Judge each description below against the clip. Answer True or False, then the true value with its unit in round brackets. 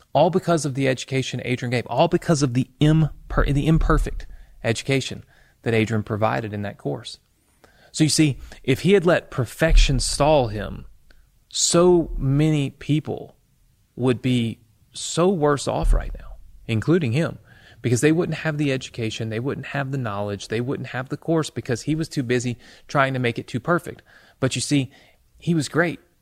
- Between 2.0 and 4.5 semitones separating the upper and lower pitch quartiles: False (5.0 semitones)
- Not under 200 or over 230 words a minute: False (175 wpm)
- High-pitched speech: False (135 Hz)